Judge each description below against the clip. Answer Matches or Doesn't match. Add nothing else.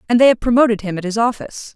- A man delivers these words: Doesn't match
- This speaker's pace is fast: Matches